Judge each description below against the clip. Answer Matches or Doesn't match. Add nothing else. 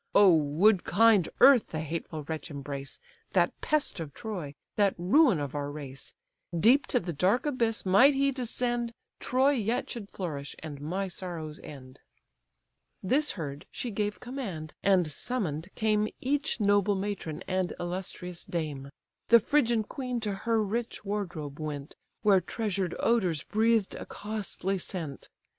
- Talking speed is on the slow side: Doesn't match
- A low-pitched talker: Doesn't match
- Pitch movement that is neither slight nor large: Doesn't match